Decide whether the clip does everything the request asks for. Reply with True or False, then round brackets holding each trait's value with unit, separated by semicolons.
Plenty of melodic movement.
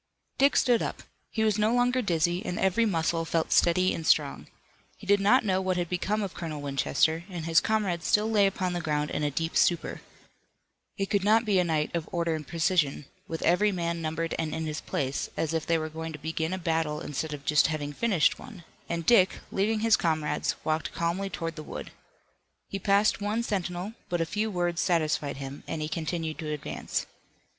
False (3.8 semitones)